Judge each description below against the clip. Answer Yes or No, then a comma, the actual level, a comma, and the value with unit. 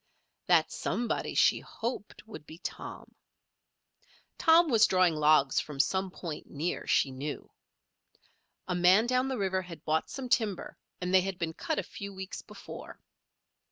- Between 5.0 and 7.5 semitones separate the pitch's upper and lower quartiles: Yes, wide, 5.6 semitones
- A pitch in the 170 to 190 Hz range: Yes, medium, 185 Hz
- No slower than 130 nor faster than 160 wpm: Yes, average, 155 wpm